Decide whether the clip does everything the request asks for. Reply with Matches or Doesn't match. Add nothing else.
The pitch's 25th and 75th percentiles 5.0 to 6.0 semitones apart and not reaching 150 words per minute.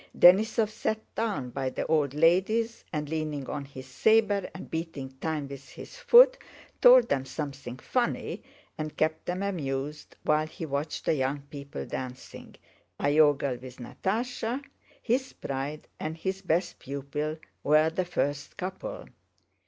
Matches